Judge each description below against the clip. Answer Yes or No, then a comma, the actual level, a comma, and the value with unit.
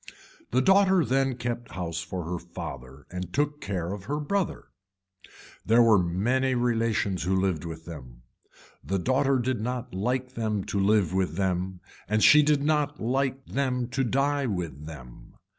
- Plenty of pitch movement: Yes, wide, 6.7 semitones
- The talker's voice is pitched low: Yes, low, 110 Hz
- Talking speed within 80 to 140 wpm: No, average, 160 wpm